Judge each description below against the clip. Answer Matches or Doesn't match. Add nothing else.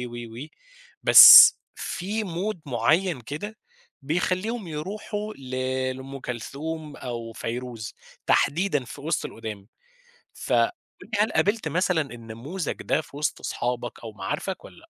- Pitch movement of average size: Doesn't match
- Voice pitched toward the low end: Doesn't match